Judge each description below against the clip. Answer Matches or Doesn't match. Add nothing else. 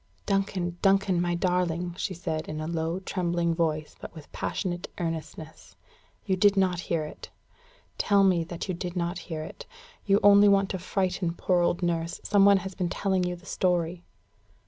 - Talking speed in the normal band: Matches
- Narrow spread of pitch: Matches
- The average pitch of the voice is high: Doesn't match